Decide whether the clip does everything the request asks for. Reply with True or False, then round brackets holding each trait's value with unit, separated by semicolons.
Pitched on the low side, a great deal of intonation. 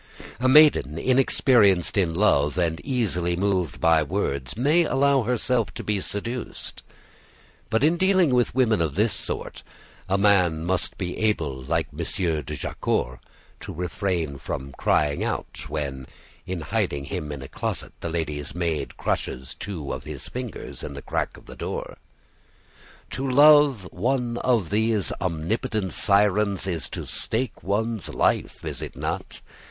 True (95 Hz; 6.7 semitones)